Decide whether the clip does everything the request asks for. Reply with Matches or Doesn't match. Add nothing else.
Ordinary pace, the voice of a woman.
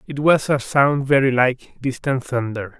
Doesn't match